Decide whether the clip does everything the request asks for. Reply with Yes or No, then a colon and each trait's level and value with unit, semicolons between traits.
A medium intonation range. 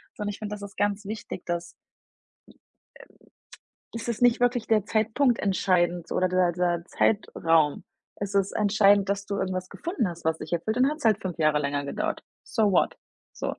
Yes: average, 3.8 semitones